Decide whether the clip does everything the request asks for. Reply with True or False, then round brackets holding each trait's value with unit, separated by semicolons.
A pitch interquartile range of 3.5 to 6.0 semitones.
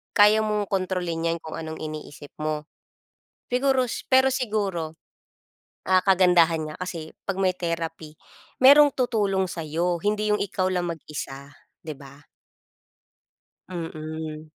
True (4.6 semitones)